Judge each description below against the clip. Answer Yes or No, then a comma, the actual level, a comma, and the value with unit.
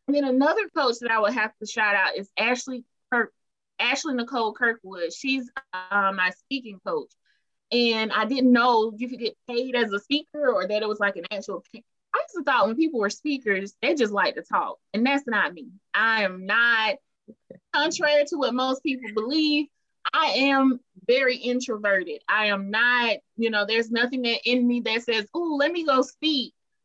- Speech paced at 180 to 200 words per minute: Yes, average, 195 wpm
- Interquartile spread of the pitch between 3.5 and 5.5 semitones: Yes, average, 4.4 semitones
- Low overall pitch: No, high, 245 Hz